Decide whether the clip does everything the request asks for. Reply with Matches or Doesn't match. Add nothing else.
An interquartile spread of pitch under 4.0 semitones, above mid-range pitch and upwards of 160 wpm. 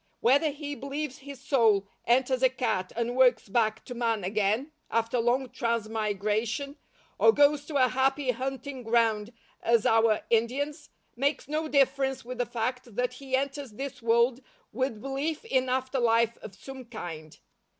Doesn't match